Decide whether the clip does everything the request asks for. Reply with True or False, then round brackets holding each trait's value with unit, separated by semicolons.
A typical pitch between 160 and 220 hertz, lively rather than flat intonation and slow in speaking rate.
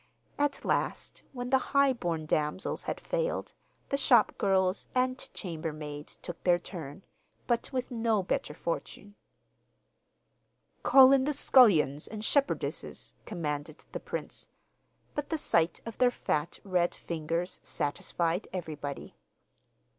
True (190 Hz; 7.9 semitones; 120 wpm)